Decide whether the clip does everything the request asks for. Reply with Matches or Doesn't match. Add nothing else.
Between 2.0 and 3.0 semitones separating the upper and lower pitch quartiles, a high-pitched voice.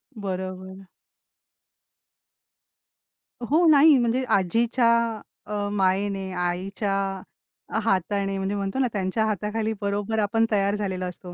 Matches